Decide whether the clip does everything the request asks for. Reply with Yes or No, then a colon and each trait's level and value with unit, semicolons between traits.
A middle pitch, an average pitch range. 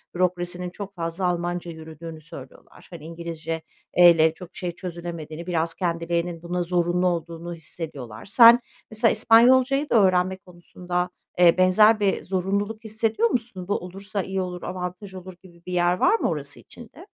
No: medium, 180 Hz; narrow, 2.2 semitones